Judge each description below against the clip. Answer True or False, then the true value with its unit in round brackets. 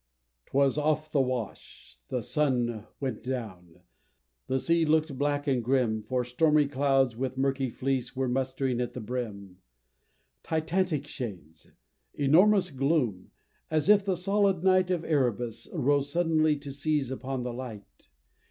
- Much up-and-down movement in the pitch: False (3.9 semitones)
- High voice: False (135 Hz)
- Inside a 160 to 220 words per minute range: False (140 wpm)